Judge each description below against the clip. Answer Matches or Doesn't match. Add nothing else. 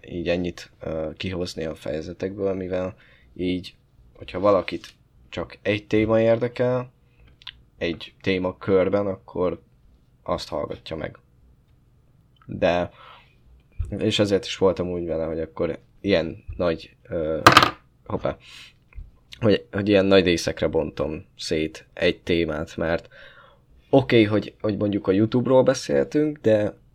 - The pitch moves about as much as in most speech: Matches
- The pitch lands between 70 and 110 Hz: Matches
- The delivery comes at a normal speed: Matches